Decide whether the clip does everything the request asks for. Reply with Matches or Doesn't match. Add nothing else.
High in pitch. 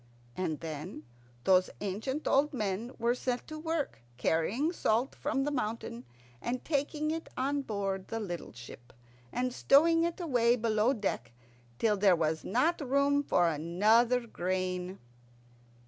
Matches